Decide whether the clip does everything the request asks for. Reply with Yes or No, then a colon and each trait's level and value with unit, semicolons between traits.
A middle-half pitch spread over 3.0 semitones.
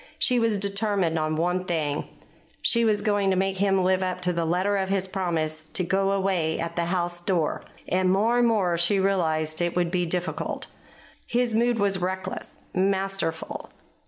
No: narrow, 2.4 semitones